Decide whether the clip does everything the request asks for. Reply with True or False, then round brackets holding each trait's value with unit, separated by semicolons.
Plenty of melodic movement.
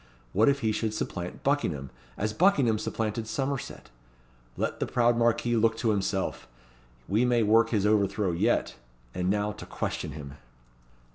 False (3.0 semitones)